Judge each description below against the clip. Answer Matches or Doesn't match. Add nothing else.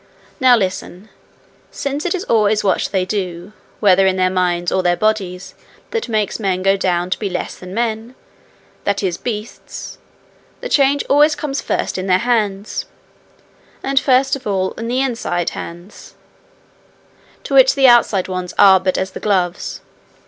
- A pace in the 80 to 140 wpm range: Doesn't match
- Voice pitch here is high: Matches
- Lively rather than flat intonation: Doesn't match